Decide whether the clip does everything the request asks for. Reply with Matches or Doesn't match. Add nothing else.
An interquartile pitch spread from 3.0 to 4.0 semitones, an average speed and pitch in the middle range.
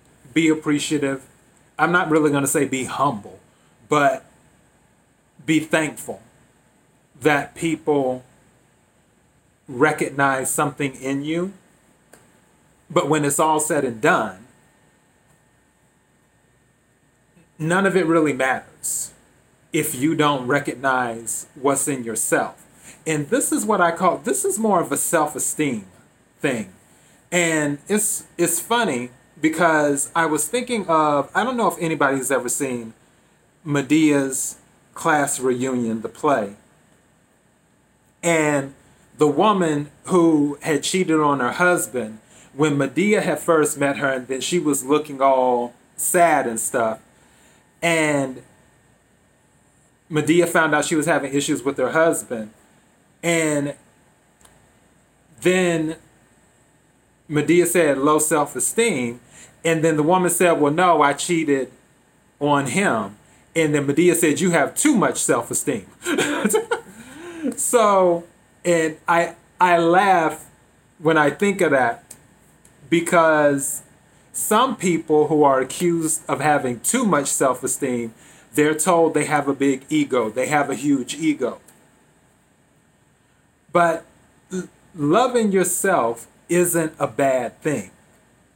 Doesn't match